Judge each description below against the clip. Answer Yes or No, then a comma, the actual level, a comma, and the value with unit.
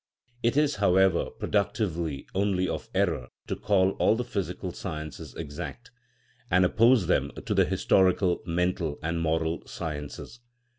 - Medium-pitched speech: No, very low, 90 Hz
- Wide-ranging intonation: No, average, 3.7 semitones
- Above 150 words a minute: No, slow, 135 wpm